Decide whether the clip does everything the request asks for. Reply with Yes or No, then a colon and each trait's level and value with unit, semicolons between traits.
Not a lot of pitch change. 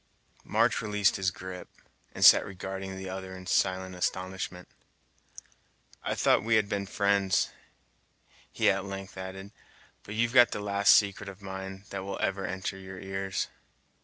Yes: narrow, 1.0 semitones